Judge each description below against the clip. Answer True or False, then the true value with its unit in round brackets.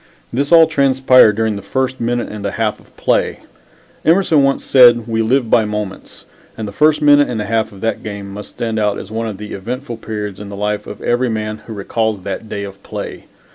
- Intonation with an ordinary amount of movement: True (3.6 semitones)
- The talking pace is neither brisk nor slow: False (220 wpm)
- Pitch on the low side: True (110 Hz)